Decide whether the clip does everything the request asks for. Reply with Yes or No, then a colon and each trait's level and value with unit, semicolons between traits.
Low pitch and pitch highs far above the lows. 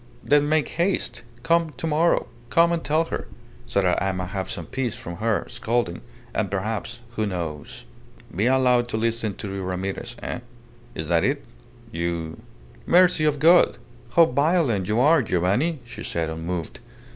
Yes: low, 115 Hz; wide, 8.7 semitones